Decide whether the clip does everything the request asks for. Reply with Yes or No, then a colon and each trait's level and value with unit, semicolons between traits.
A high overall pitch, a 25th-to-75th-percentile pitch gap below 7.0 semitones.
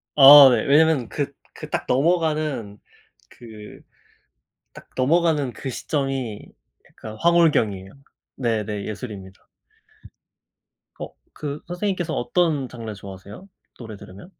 No: low, 130 Hz; wide, 6.3 semitones